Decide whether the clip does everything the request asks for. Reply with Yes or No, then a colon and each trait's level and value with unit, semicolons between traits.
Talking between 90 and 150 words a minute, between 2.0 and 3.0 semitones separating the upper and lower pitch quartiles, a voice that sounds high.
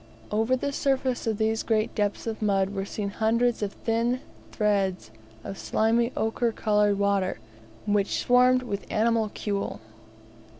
Yes: slow, 135 wpm; narrow, 2.5 semitones; high, 220 Hz